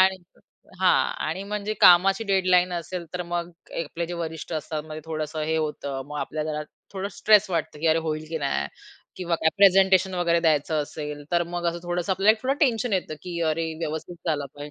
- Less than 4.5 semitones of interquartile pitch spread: Yes, average, 3.3 semitones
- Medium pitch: Yes, medium, 170 Hz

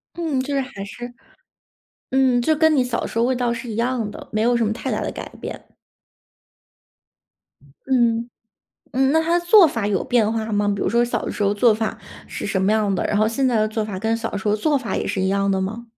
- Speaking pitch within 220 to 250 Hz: Yes, high, 230 Hz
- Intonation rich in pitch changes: No, average, 3.5 semitones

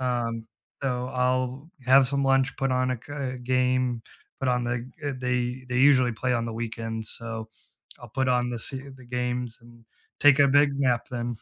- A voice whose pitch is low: Yes, low, 125 Hz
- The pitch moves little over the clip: Yes, narrow, 1.4 semitones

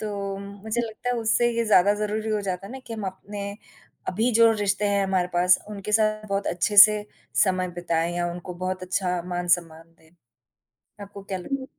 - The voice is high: Yes, high, 200 Hz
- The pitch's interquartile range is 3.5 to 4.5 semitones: No, average, 2.9 semitones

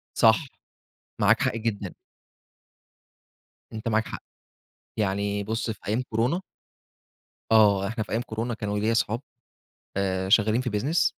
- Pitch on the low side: Yes, low, 110 Hz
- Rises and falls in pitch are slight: Yes, narrow, 2.1 semitones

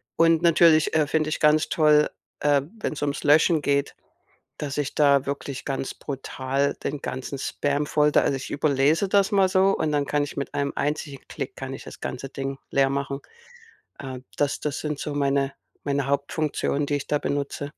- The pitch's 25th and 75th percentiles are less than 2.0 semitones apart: Yes, narrow, 1.6 semitones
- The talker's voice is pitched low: No, medium, 145 Hz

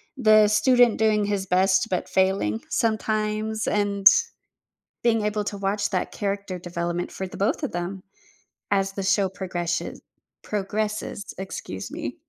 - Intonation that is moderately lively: No, narrow, 2.1 semitones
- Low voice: No, high, 200 Hz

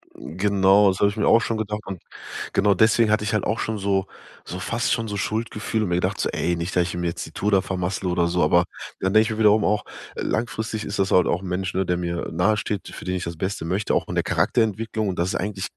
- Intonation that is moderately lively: Yes, average, 3.0 semitones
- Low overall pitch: Yes, low, 100 Hz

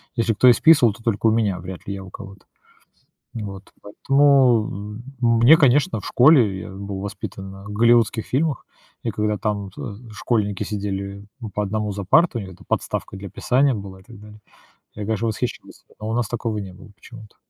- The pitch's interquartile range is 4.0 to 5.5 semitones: No, average, 3.0 semitones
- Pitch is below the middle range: Yes, low, 105 Hz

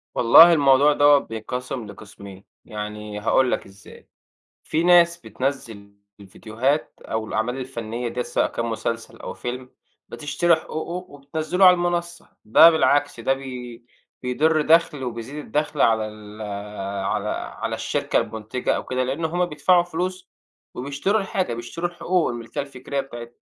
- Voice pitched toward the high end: No, low, 135 Hz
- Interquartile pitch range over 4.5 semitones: Yes, wide, 5.6 semitones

